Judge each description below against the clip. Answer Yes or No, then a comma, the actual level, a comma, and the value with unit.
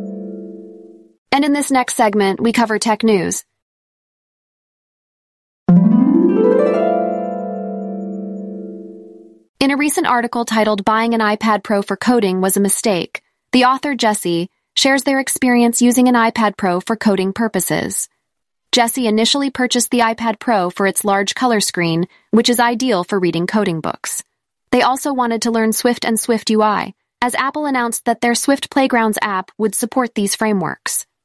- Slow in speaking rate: No, average, 145 wpm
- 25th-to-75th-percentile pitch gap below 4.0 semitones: Yes, average, 3.5 semitones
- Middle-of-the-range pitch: No, high, 225 Hz